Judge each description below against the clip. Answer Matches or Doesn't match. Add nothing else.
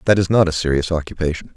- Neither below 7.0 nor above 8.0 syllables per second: Matches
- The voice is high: Doesn't match